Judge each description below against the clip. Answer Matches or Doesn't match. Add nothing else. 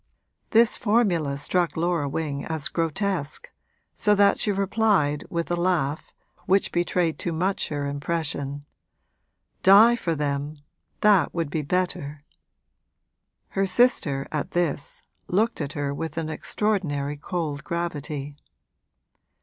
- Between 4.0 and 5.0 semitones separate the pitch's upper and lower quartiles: Matches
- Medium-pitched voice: Matches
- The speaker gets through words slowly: Matches